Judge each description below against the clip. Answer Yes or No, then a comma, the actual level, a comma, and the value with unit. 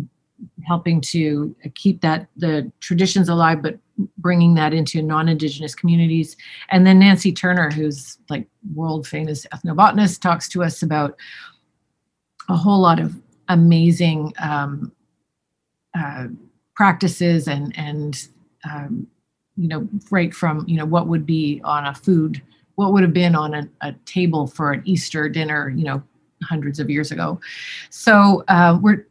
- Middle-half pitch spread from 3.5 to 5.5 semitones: No, average, 3.1 semitones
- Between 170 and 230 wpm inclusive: No, average, 145 wpm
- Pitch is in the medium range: Yes, medium, 165 Hz